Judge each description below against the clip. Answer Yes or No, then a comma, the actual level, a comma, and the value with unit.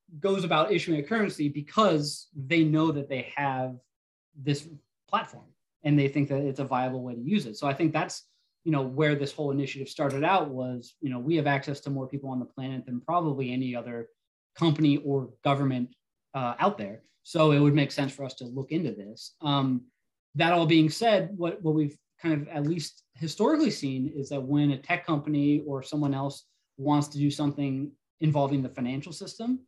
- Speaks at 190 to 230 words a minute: Yes, average, 200 wpm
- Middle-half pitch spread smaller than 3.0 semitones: Yes, narrow, 2.6 semitones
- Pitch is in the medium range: Yes, medium, 145 Hz